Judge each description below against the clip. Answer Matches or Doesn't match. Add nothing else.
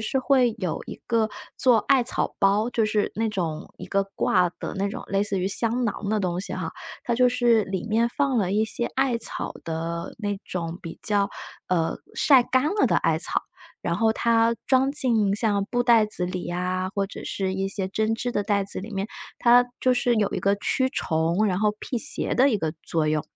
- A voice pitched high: Matches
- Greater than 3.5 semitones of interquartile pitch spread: Matches